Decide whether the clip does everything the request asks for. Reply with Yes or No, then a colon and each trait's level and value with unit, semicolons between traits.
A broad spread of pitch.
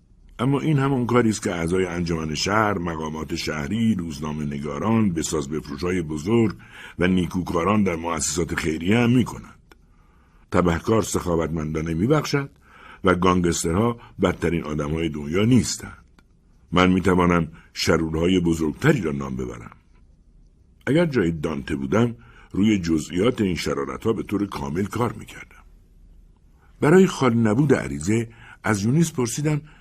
Yes: wide, 6.0 semitones